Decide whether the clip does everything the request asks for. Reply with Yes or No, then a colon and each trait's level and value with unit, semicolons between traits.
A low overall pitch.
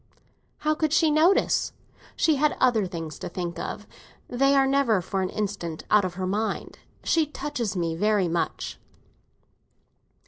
No: high, 215 Hz